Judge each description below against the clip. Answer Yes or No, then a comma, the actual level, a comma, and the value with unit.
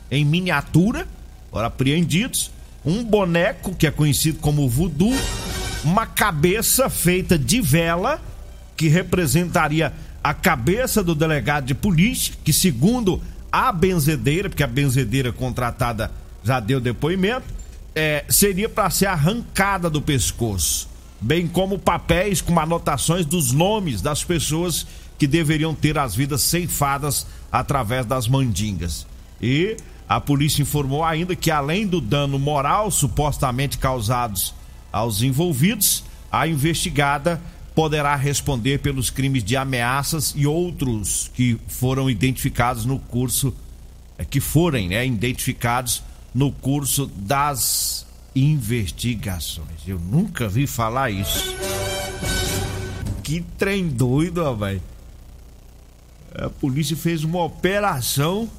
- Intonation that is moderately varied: No, wide, 6.1 semitones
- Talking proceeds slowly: Yes, slow, 115 wpm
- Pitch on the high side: No, medium, 140 Hz